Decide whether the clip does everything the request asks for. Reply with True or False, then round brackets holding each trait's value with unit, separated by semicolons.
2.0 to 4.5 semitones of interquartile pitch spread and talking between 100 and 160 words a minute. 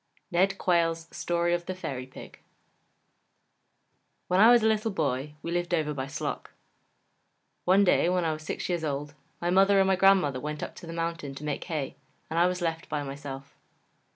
False (3.6 semitones; 185 wpm)